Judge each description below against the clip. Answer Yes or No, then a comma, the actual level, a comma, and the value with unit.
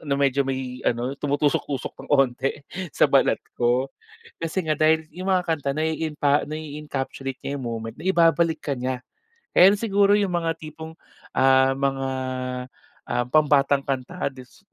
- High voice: No, medium, 145 Hz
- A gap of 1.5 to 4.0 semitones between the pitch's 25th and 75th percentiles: Yes, average, 3.3 semitones